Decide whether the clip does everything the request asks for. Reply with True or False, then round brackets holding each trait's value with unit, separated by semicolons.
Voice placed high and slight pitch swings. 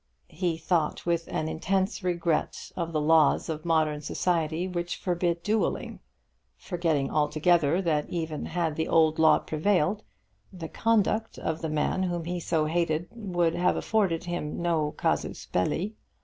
False (170 Hz; 2.2 semitones)